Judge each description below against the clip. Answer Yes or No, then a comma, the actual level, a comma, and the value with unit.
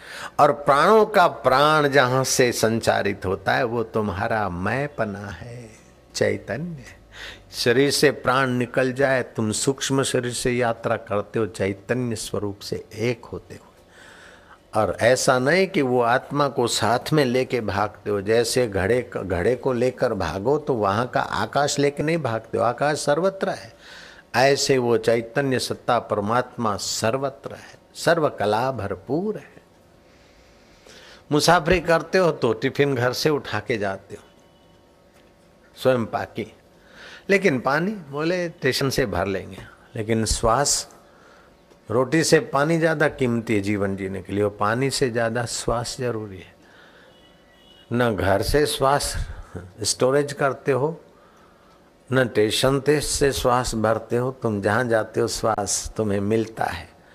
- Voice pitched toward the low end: Yes, low, 120 Hz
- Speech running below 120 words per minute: No, average, 140 wpm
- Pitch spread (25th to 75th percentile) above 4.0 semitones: Yes, average, 4.5 semitones